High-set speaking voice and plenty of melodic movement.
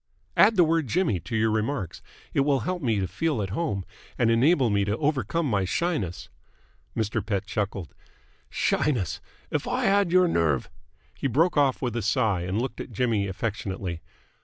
No: low, 115 Hz; wide, 7.0 semitones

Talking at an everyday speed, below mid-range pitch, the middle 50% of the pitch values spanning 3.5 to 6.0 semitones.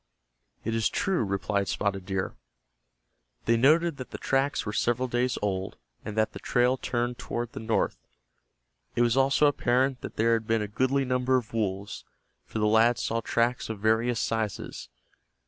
No: average, 170 wpm; low, 115 Hz; average, 2.9 semitones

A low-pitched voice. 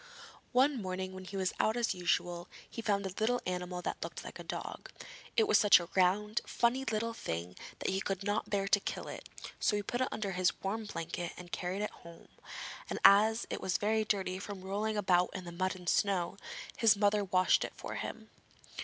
No: high, 195 Hz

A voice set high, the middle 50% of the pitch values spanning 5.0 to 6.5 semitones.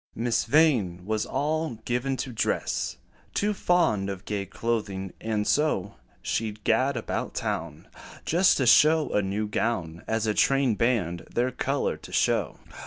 No: low, 115 Hz; average, 5.3 semitones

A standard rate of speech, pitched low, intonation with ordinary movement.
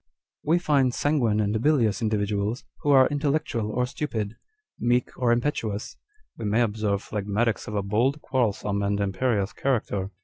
Yes: average, 150 wpm; low, 115 Hz; average, 4.2 semitones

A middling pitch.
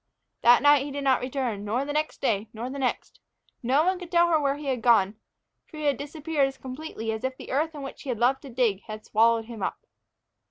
No: very high, 265 Hz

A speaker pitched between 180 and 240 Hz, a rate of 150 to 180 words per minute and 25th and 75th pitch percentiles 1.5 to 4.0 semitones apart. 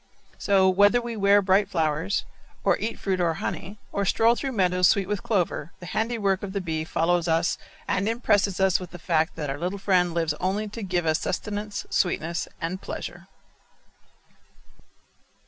Yes: high, 190 Hz; average, 170 wpm; average, 2.9 semitones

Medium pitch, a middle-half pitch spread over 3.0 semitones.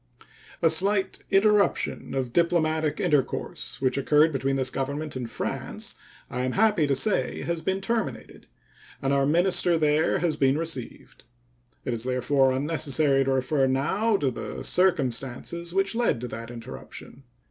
Yes: medium, 150 Hz; average, 4.6 semitones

